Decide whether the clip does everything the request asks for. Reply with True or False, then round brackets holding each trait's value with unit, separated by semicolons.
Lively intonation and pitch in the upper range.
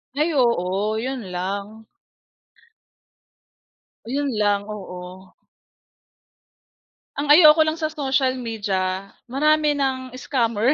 True (6.0 semitones; 235 Hz)